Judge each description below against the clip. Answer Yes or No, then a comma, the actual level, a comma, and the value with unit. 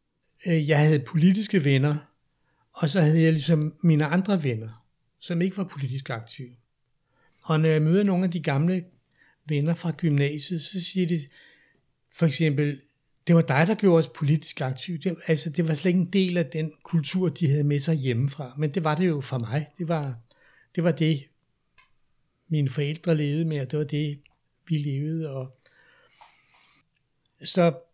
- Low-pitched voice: No, medium, 155 Hz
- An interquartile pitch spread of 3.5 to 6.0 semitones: No, average, 3.0 semitones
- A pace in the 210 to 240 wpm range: No, average, 175 wpm